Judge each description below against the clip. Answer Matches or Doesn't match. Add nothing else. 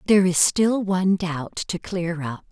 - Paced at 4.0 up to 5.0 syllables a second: Matches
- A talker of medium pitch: Matches